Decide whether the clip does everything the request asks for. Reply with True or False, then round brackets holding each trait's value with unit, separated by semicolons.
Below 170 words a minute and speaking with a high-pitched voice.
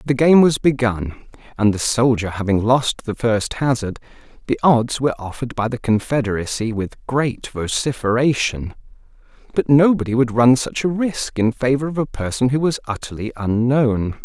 False (160 wpm; 120 Hz)